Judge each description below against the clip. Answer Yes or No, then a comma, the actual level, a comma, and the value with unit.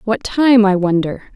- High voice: Yes, high, 210 Hz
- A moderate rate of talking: Yes, average, 175 wpm